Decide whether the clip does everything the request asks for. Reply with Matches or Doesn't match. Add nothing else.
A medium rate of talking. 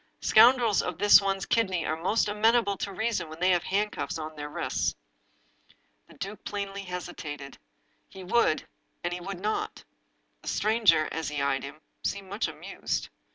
Matches